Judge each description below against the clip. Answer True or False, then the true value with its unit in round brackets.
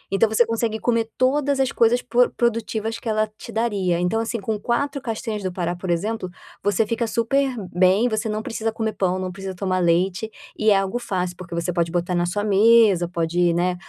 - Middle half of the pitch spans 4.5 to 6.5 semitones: False (4.0 semitones)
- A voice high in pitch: True (215 Hz)